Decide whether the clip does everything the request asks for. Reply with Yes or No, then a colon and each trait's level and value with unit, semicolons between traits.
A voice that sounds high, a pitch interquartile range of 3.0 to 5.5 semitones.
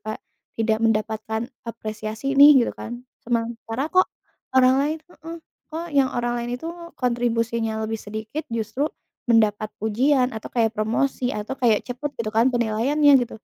Yes: high, 235 Hz; average, 3.3 semitones